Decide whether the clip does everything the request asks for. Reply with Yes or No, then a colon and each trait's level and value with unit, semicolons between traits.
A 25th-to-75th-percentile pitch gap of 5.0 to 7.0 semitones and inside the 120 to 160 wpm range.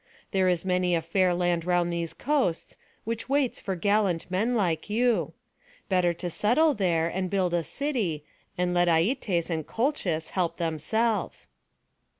No: average, 4.3 semitones; average, 155 wpm